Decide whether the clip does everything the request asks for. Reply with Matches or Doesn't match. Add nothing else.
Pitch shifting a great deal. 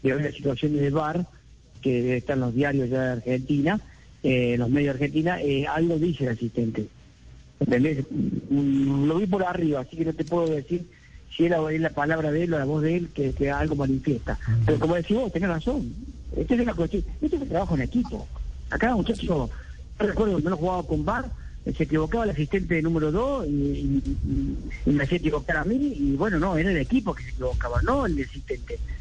Doesn't match